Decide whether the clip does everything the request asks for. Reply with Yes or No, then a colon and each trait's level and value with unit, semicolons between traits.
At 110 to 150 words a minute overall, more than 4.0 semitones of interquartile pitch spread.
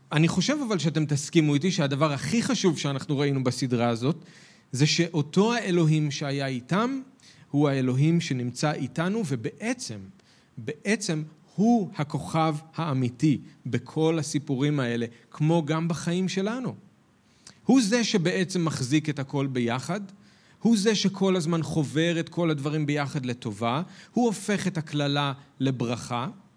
Yes: average, 125 wpm; average, 4.4 semitones